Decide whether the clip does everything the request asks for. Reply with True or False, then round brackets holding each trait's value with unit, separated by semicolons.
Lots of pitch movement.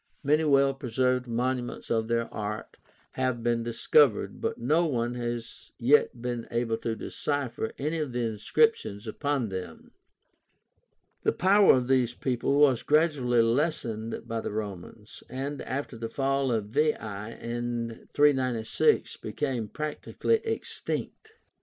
False (3.8 semitones)